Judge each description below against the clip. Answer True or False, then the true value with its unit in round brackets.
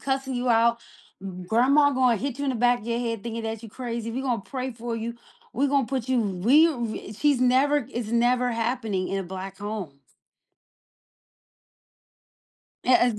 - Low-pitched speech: False (235 Hz)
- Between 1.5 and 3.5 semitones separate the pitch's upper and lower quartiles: True (2.8 semitones)